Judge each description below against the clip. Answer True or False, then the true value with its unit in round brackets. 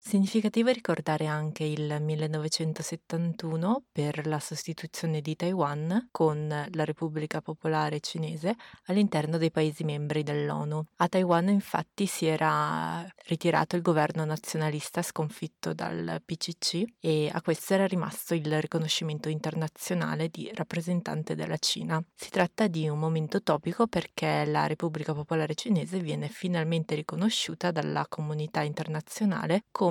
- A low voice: False (160 Hz)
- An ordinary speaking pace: True (125 wpm)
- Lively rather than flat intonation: False (2.4 semitones)